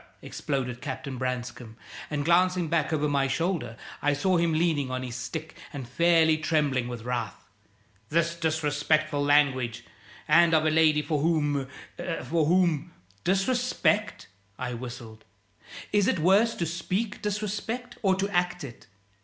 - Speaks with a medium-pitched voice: Yes, medium, 155 Hz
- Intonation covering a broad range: No, average, 4.8 semitones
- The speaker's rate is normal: Yes, average, 145 wpm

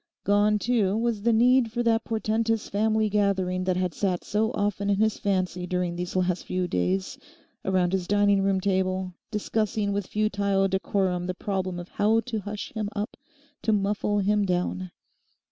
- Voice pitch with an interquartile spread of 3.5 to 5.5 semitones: No, narrow, 2.5 semitones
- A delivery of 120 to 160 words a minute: No, average, 170 wpm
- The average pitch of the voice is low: No, high, 200 Hz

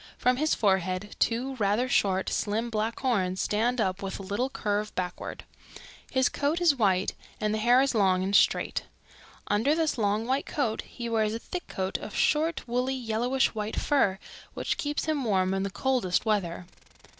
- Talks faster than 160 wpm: Yes, average, 180 wpm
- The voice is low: No, high, 220 Hz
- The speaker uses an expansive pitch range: No, average, 4.7 semitones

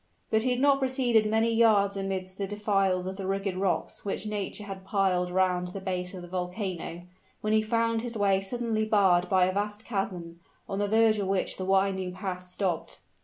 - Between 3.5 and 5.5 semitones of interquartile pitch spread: No, average, 2.7 semitones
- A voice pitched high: Yes, high, 195 Hz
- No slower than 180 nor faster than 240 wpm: Yes, average, 200 wpm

